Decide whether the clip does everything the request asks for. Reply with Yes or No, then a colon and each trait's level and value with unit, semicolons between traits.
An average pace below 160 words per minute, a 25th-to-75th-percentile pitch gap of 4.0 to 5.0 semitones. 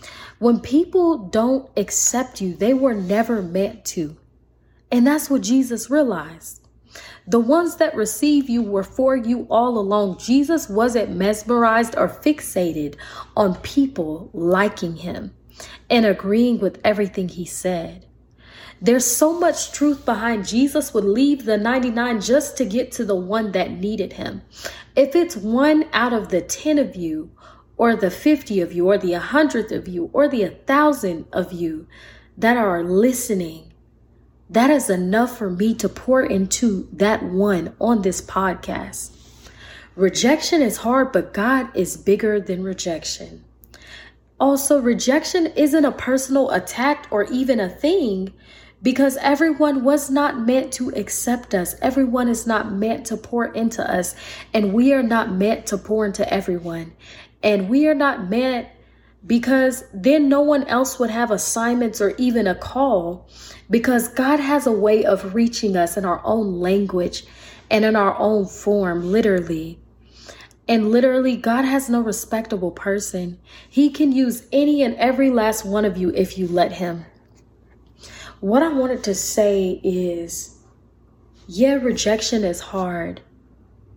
No: average, 150 wpm; wide, 5.4 semitones